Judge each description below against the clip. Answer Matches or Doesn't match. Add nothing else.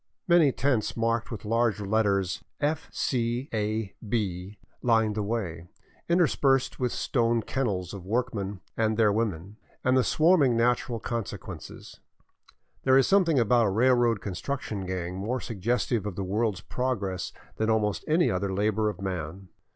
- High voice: Doesn't match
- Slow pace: Doesn't match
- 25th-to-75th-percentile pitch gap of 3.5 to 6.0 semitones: Matches